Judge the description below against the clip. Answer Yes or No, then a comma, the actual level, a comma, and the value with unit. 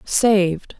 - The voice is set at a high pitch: Yes, high, 195 Hz